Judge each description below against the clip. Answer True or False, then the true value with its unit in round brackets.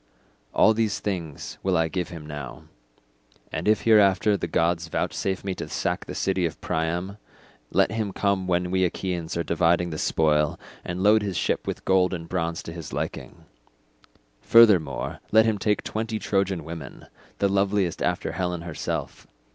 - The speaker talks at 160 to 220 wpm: True (165 wpm)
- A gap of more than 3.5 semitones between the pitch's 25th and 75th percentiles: False (3.2 semitones)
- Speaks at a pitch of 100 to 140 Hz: False (90 Hz)